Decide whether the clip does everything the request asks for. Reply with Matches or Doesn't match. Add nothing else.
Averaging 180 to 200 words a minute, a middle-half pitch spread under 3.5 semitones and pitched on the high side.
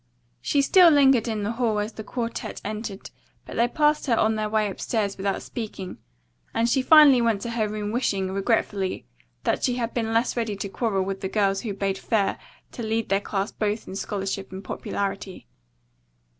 Matches